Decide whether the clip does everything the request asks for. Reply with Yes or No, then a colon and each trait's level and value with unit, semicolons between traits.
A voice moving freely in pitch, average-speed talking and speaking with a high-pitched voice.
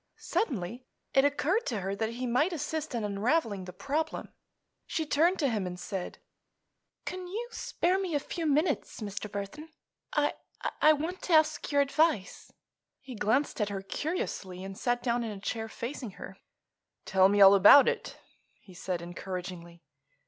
Yes: wide, 7.9 semitones; average, 165 wpm; high, 240 Hz